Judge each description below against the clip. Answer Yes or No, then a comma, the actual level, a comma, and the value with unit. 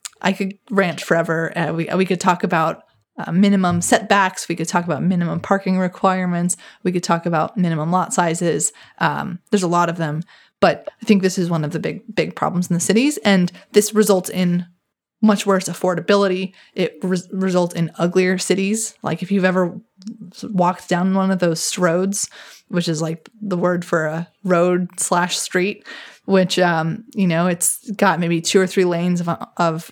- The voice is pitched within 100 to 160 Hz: No, medium, 180 Hz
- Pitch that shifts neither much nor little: No, narrow, 2.2 semitones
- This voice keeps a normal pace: Yes, average, 185 wpm